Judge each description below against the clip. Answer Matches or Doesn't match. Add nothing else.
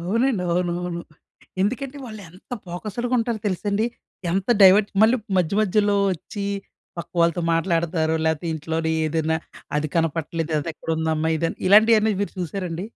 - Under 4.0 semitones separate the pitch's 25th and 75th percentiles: Doesn't match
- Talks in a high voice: Doesn't match